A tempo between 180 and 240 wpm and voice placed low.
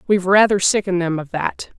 No: average, 200 wpm; medium, 185 Hz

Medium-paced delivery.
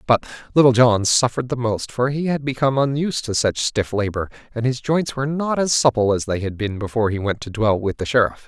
No: fast, 240 wpm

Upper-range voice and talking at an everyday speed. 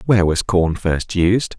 No: very low, 95 Hz; average, 190 wpm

